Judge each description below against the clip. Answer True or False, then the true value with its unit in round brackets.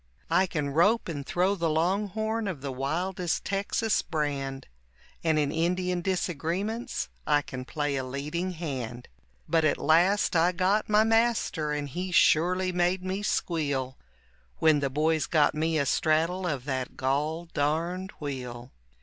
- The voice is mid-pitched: True (165 Hz)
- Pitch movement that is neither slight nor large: True (4.3 semitones)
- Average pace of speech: True (150 wpm)